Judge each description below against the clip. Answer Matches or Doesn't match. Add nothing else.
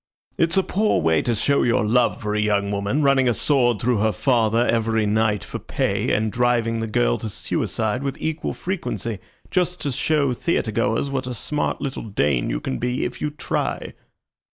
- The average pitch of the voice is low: Matches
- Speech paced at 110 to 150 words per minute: Doesn't match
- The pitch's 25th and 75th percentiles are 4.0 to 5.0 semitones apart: Matches